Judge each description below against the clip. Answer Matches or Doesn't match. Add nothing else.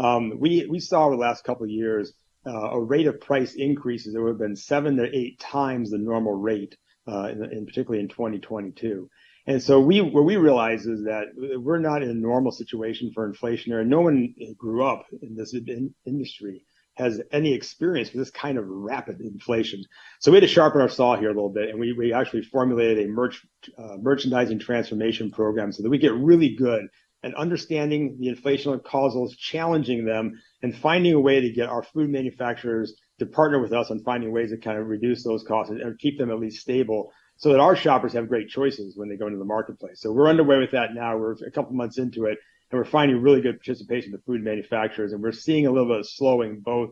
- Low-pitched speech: Matches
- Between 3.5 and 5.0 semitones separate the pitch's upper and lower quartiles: Matches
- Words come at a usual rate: Doesn't match